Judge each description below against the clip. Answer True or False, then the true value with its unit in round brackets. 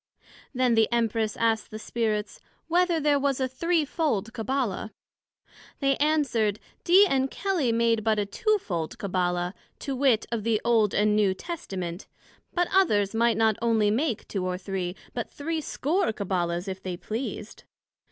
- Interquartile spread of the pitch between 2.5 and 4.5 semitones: False (5.5 semitones)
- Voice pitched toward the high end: True (225 Hz)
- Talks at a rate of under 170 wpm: True (150 wpm)